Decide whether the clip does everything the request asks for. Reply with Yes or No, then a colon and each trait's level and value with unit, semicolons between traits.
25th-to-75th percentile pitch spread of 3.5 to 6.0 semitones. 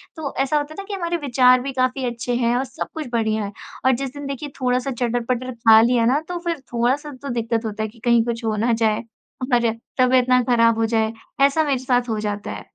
No: average, 2.9 semitones